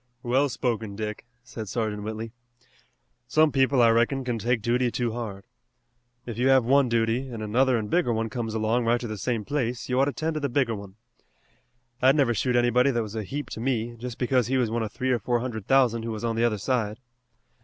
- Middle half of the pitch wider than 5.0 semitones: No, narrow, 2.5 semitones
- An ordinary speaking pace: No, fast, 230 wpm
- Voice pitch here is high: No, low, 120 Hz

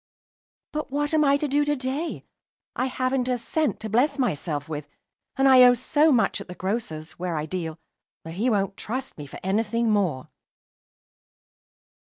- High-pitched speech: Yes, high, 235 Hz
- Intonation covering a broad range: Yes, wide, 6.8 semitones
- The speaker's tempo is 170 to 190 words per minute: Yes, average, 180 wpm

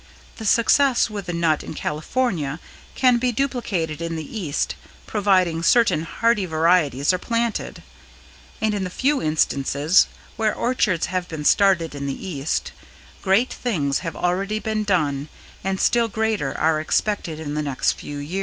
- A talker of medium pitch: Yes, medium, 180 Hz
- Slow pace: No, average, 155 wpm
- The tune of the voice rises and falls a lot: Yes, wide, 5.9 semitones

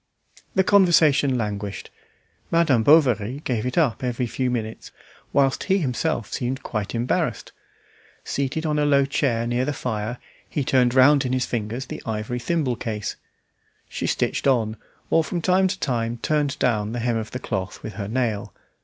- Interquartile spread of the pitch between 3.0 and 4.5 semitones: Yes, average, 4.2 semitones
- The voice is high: No, low, 125 Hz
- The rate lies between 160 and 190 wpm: Yes, average, 170 wpm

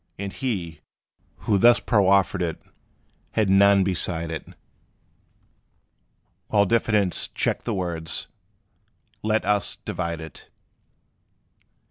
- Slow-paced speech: Yes, slow, 95 wpm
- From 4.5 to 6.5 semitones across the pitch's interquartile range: No, average, 3.6 semitones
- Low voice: Yes, very low, 95 Hz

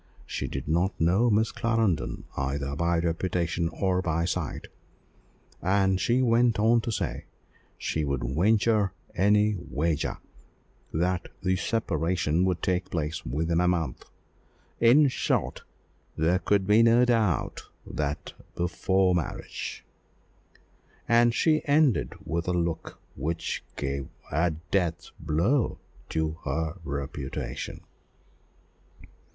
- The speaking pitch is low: Yes, very low, 90 Hz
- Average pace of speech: No, slow, 115 wpm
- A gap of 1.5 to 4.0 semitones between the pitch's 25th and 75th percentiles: No, average, 4.8 semitones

